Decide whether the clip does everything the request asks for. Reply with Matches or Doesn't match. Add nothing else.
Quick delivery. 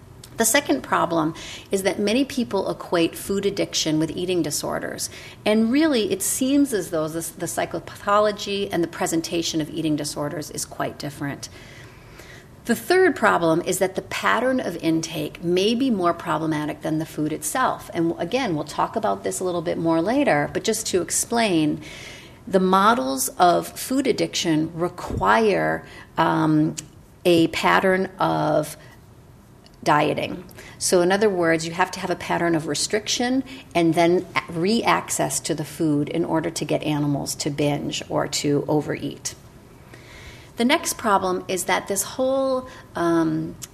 Doesn't match